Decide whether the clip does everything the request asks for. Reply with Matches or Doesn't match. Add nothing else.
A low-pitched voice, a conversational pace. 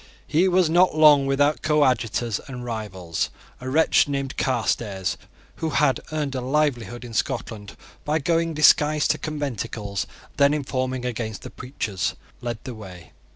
Matches